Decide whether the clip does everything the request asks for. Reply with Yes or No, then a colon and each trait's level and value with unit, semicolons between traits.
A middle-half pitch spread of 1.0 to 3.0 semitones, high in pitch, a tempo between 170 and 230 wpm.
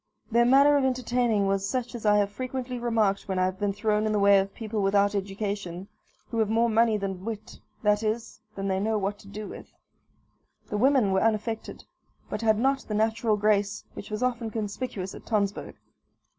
Yes: narrow, 2.5 semitones; high, 215 Hz; average, 200 wpm